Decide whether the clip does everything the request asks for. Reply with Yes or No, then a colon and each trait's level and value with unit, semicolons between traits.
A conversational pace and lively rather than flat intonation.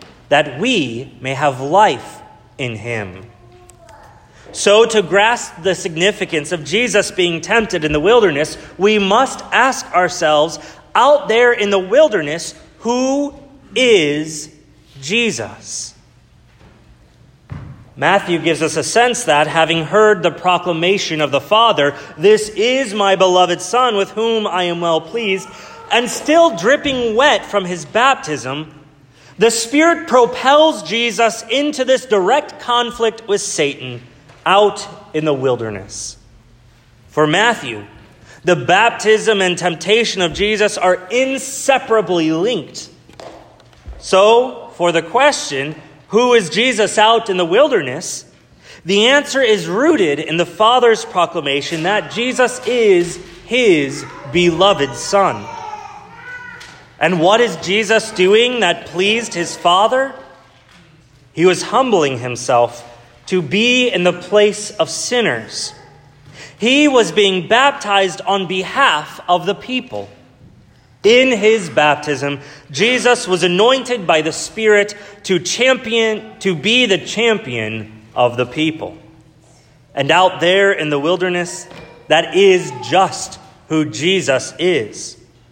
No: slow, 120 wpm; wide, 7.1 semitones